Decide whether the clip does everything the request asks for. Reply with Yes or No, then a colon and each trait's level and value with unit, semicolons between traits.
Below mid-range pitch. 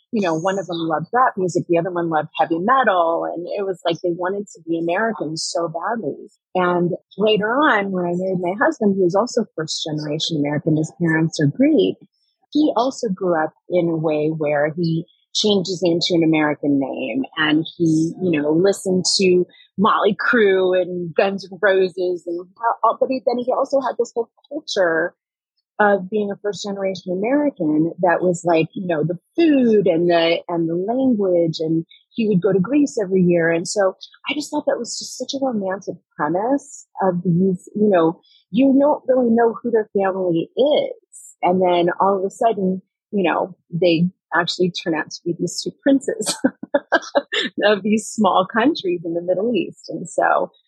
No: medium, 185 Hz